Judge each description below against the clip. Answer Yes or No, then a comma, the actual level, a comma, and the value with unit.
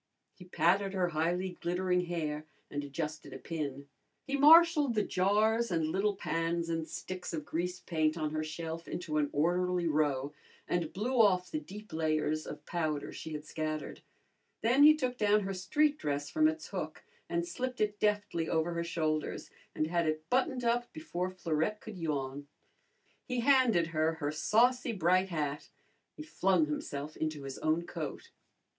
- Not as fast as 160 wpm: No, average, 165 wpm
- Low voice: No, medium, 175 Hz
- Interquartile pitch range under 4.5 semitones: No, average, 5.3 semitones